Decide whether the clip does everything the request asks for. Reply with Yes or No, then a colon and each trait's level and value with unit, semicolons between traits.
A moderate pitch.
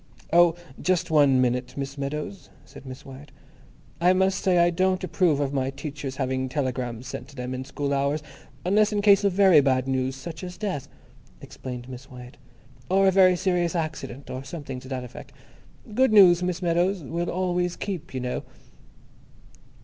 Yes: medium, 150 Hz